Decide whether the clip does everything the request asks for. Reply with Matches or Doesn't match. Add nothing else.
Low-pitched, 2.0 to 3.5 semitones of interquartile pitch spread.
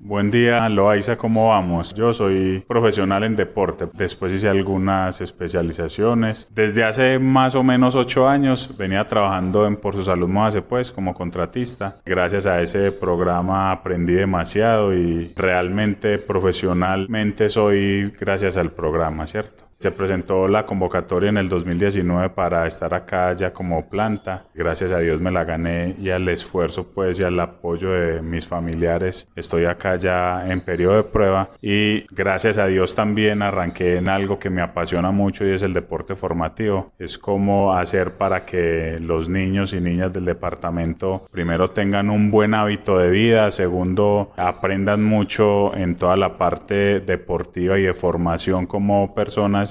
Matches